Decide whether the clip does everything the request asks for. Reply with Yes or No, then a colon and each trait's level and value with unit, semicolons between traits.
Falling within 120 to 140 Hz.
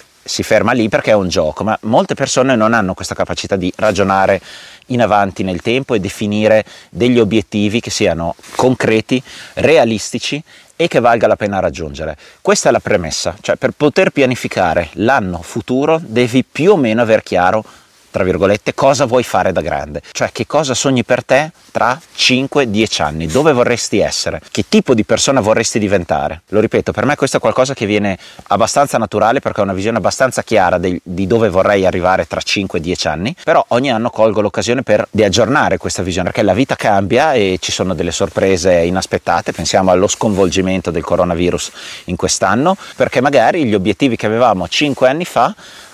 No: low, 110 Hz